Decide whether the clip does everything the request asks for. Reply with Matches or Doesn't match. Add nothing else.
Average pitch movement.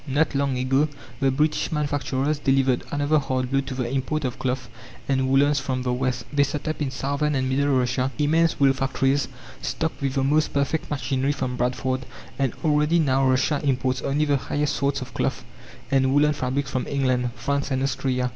Doesn't match